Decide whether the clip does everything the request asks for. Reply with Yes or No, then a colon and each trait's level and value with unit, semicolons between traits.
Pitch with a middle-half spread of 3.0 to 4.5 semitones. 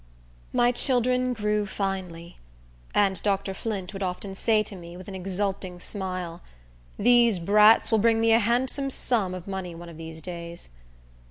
Yes: average, 3.7 semitones